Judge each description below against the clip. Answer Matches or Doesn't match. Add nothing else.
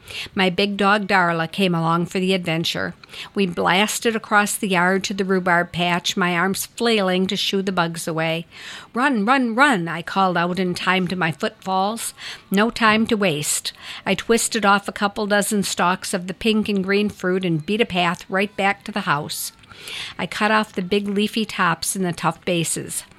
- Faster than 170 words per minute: Matches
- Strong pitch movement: Doesn't match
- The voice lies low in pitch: Doesn't match